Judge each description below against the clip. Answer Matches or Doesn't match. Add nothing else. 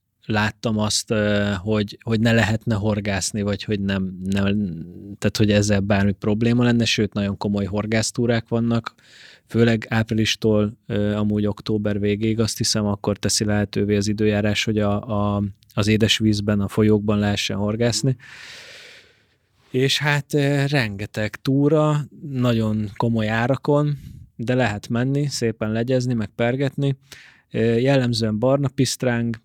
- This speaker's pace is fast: Doesn't match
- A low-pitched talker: Matches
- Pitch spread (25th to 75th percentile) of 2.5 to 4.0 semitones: Matches